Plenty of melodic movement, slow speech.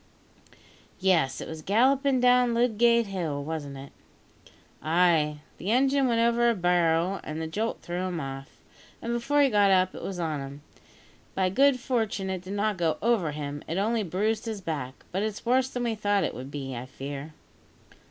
No: wide, 6.9 semitones; average, 185 wpm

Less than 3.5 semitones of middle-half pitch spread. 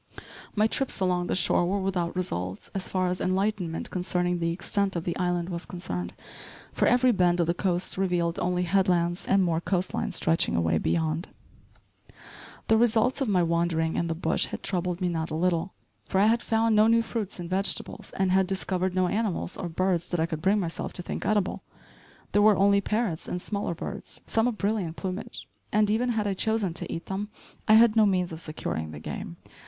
Yes: average, 3.1 semitones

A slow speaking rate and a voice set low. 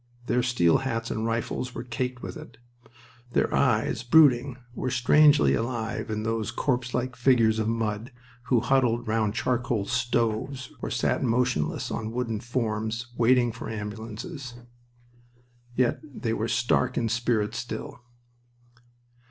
Yes: slow, 130 wpm; low, 120 Hz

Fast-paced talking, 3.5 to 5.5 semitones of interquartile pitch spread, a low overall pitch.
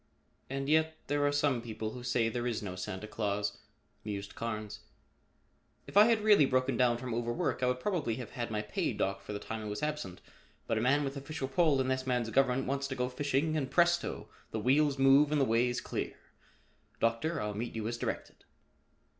Yes: fast, 210 wpm; average, 4.2 semitones; low, 125 Hz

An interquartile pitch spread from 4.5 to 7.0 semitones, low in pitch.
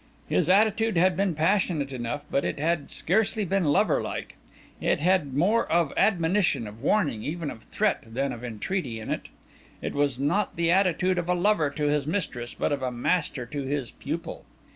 No: wide, 5.4 semitones; medium, 160 Hz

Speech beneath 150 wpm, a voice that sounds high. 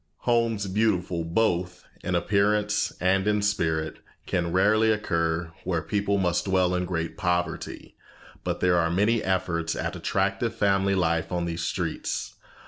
No: average, 140 wpm; very low, 95 Hz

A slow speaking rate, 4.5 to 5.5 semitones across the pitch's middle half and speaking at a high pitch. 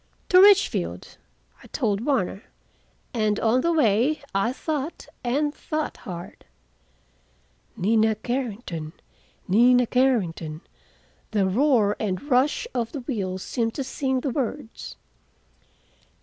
Yes: slow, 110 wpm; average, 5.0 semitones; high, 240 Hz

